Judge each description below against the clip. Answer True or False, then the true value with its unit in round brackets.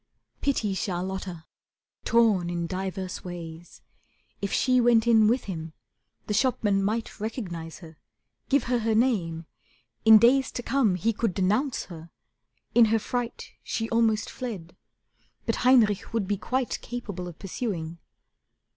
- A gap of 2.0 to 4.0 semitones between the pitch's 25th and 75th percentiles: False (4.8 semitones)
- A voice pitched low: False (210 Hz)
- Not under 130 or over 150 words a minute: True (140 wpm)